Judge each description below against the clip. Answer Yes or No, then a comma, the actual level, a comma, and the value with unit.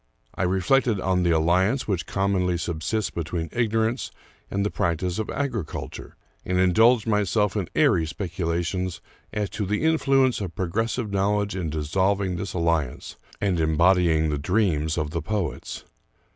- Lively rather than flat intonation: No, average, 3.8 semitones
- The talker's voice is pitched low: Yes, very low, 95 Hz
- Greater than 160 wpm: No, average, 155 wpm